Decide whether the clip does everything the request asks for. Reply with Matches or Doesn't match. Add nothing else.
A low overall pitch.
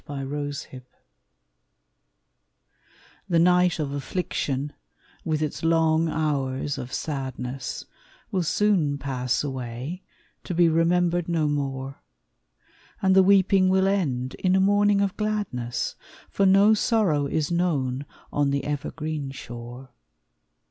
Doesn't match